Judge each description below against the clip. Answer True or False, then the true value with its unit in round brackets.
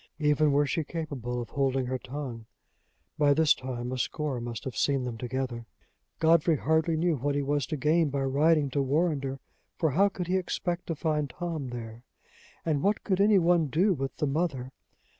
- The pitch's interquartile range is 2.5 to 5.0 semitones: True (3.8 semitones)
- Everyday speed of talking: True (190 wpm)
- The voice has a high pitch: False (145 Hz)